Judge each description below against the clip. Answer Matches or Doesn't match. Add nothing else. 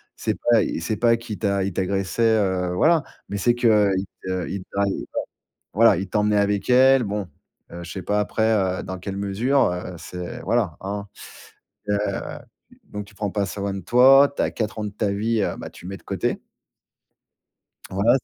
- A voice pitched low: Matches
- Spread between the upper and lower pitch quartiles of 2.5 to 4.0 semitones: Matches